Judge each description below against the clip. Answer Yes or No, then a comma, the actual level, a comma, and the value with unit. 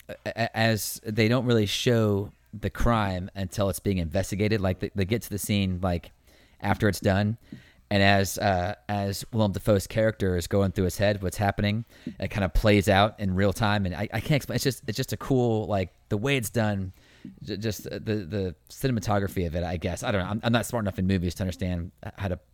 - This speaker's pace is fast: Yes, fast, 215 wpm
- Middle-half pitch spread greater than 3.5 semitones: No, narrow, 2.6 semitones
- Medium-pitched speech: No, low, 100 Hz